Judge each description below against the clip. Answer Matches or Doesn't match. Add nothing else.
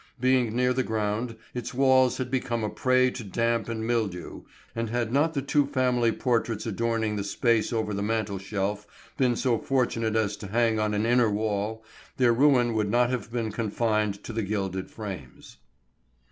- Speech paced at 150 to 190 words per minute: Matches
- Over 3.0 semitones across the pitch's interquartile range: Doesn't match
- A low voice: Matches